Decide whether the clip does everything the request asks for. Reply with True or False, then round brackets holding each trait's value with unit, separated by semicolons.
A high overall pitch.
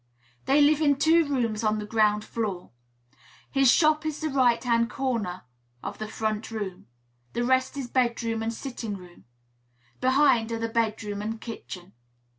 True (230 Hz)